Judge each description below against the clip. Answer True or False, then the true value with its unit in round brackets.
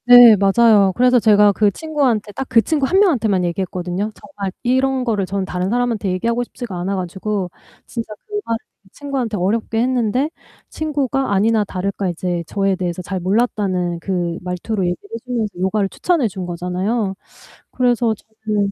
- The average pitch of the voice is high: True (210 Hz)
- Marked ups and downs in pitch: False (4.5 semitones)